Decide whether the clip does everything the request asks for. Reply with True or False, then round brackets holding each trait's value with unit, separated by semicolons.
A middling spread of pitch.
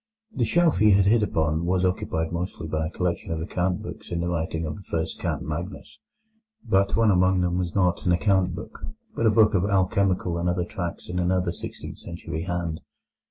False (2.3 semitones)